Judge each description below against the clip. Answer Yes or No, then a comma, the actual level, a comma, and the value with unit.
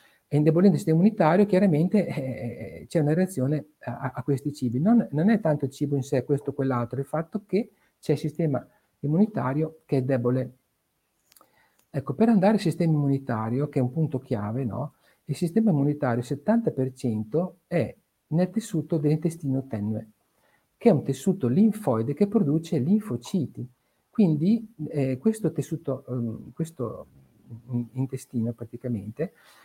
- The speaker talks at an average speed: Yes, average, 150 wpm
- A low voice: No, medium, 145 Hz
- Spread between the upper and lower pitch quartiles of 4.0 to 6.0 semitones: Yes, average, 5.2 semitones